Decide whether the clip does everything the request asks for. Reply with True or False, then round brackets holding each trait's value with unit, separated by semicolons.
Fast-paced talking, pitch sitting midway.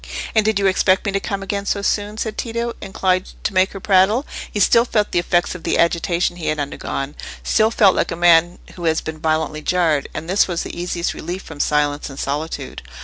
True (215 wpm; 180 Hz)